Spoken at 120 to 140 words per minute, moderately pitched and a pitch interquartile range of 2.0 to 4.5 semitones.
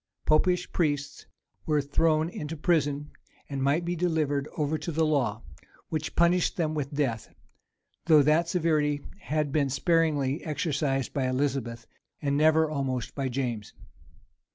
Yes: slow, 135 wpm; medium, 150 Hz; narrow, 2.6 semitones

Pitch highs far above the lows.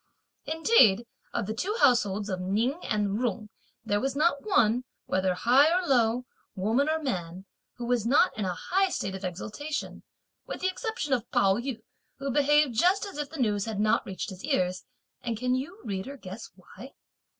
Yes: wide, 6.2 semitones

